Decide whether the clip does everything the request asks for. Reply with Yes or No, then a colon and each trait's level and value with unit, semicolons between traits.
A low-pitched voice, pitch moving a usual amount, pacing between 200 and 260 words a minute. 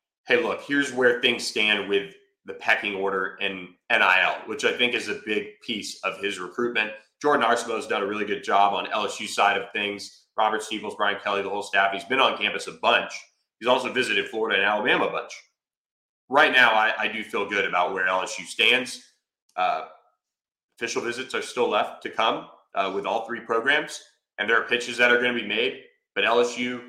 Yes: low, 110 Hz; average, 3.9 semitones; fast, 205 wpm